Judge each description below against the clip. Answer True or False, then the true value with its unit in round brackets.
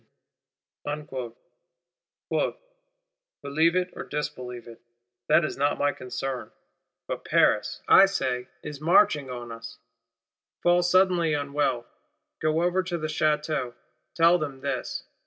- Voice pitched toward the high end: False (150 Hz)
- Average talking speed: False (115 wpm)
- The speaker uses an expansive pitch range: False (4.9 semitones)